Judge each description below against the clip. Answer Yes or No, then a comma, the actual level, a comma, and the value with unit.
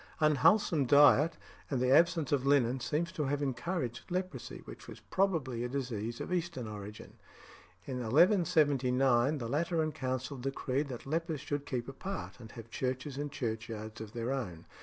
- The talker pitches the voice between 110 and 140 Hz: Yes, low, 135 Hz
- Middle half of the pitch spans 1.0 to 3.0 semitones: No, average, 4.2 semitones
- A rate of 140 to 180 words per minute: Yes, average, 160 wpm